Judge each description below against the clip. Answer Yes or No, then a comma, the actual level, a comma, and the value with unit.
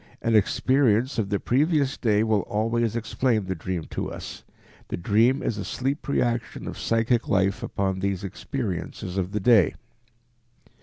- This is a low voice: Yes, low, 110 Hz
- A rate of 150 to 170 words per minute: Yes, average, 155 wpm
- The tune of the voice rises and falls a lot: No, average, 3.8 semitones